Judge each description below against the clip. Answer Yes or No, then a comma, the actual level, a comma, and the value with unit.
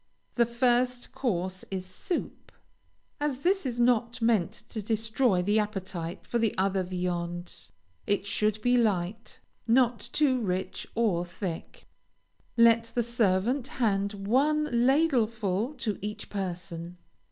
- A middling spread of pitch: Yes, average, 4.5 semitones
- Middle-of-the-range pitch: No, high, 220 Hz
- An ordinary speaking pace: No, slow, 120 wpm